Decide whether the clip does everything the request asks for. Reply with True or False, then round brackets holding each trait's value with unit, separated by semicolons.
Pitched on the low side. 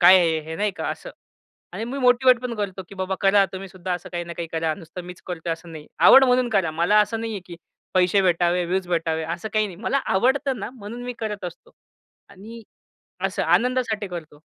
False (190 Hz)